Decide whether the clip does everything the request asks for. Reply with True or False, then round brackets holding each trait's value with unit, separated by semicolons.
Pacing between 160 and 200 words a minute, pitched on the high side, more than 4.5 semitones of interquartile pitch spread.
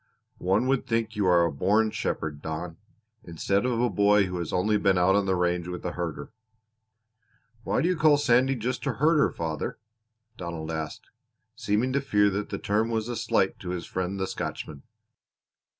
False (180 wpm; 100 Hz; 4.9 semitones)